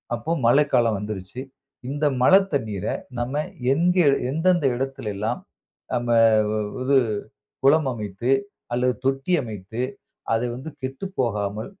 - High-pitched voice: No, low, 125 Hz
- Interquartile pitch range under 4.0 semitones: No, average, 4.4 semitones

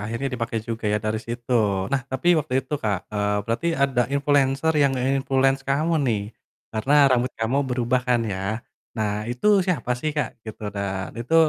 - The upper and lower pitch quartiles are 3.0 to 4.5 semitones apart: Yes, average, 3.9 semitones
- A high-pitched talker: No, low, 125 Hz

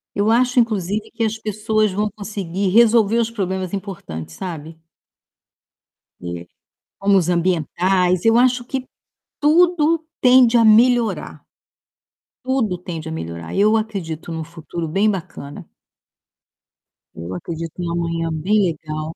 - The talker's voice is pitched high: Yes, high, 195 Hz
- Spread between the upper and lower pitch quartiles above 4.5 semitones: Yes, average, 4.9 semitones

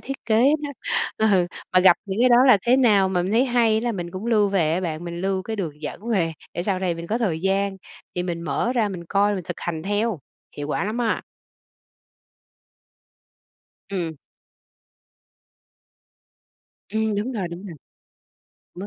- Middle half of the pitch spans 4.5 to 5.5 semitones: No, average, 4.1 semitones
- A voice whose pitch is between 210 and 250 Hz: No, high, 195 Hz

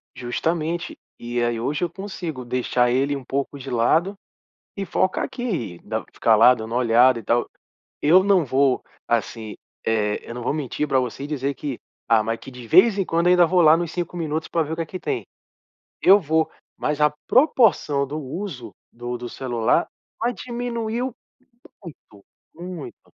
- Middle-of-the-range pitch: Yes, medium, 145 Hz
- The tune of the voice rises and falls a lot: Yes, wide, 6.4 semitones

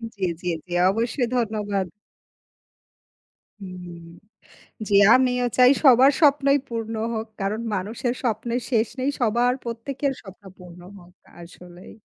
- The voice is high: Yes, high, 225 Hz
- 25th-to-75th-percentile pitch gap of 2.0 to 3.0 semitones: No, average, 4.3 semitones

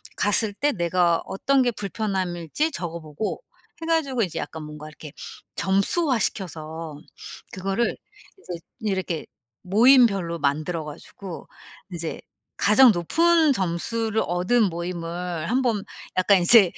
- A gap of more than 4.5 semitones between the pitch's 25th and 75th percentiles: Yes, average, 5.3 semitones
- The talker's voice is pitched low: No, high, 190 Hz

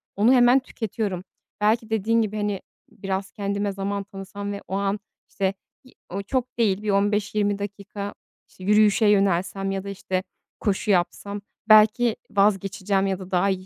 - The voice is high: Yes, high, 200 Hz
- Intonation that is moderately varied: No, narrow, 1.6 semitones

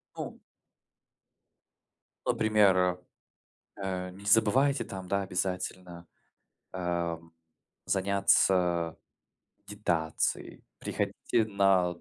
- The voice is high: No, very low, 95 Hz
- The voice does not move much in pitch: Yes, narrow, 2.3 semitones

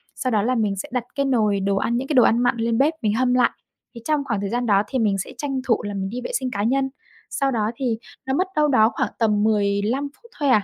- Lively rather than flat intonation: No, average, 4.2 semitones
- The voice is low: No, high, 235 Hz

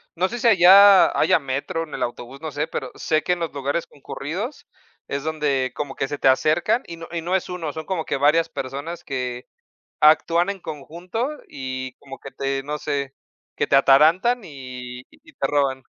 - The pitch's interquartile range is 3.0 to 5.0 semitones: Yes, average, 4.2 semitones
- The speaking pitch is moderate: Yes, medium, 150 Hz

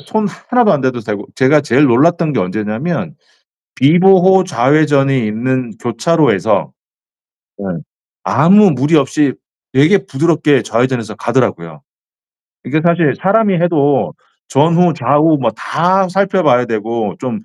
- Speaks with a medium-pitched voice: Yes, medium, 145 Hz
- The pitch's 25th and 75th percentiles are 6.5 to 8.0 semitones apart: No, wide, 5.8 semitones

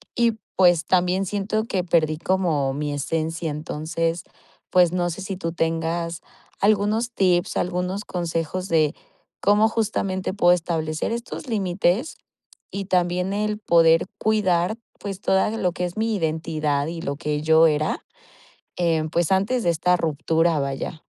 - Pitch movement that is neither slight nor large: Yes, average, 3.2 semitones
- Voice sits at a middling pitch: Yes, medium, 175 Hz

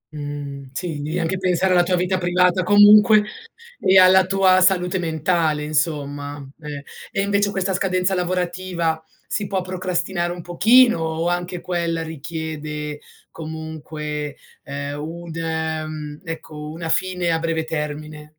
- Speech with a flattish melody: No, average, 3.2 semitones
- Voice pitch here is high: No, medium, 165 Hz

